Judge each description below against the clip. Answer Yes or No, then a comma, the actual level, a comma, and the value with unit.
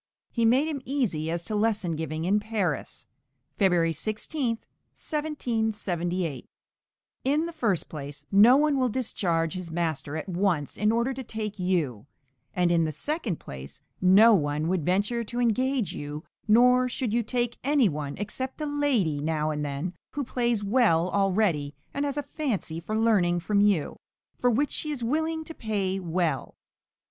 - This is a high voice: Yes, high, 205 Hz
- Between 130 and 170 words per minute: Yes, average, 165 wpm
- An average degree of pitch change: No, wide, 6.9 semitones